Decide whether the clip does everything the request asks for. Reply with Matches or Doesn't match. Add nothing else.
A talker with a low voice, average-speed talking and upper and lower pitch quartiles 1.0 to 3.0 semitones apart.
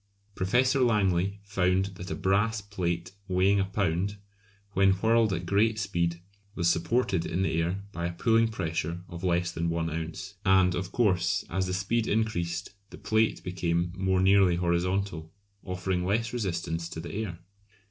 Matches